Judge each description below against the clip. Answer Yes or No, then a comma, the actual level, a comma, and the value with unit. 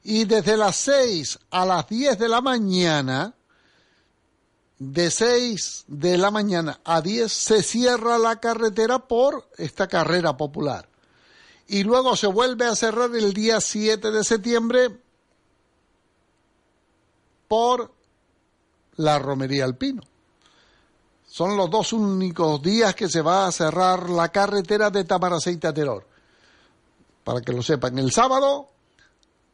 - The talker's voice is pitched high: Yes, high, 205 Hz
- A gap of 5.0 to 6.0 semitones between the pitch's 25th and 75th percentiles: Yes, wide, 5.4 semitones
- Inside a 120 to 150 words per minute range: Yes, slow, 125 wpm